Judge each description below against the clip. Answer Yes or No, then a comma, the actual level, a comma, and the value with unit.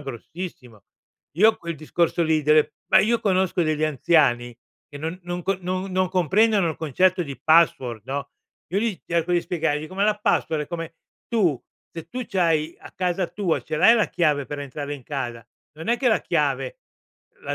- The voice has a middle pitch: Yes, medium, 170 Hz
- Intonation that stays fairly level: No, average, 4.1 semitones